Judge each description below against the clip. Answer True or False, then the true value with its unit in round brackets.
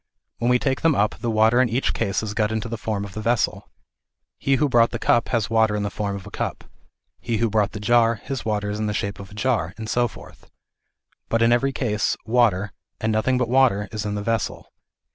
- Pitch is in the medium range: False (110 Hz)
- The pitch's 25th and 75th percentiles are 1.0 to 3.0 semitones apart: True (2.5 semitones)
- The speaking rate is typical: False (240 wpm)